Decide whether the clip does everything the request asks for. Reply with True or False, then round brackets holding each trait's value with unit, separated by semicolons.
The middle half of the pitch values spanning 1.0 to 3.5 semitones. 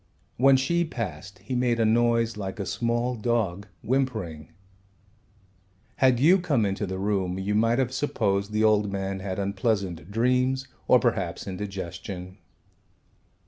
False (4.2 semitones)